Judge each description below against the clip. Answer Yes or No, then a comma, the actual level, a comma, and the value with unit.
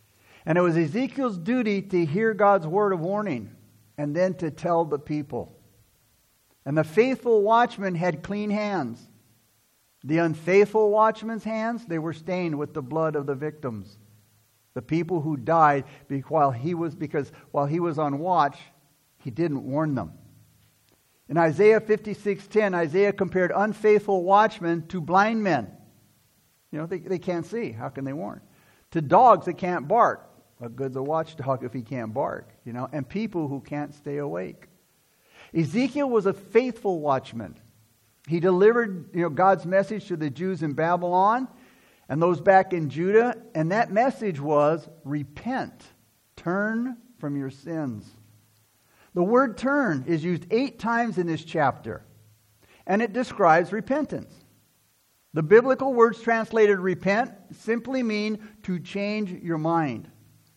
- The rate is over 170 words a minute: No, average, 150 wpm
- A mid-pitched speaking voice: Yes, medium, 170 Hz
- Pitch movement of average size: No, wide, 6.5 semitones